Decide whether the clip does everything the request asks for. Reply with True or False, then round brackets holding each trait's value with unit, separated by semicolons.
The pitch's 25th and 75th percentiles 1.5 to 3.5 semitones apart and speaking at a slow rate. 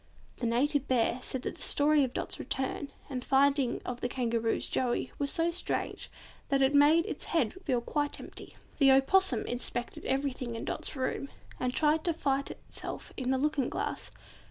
False (2.7 semitones; 180 wpm)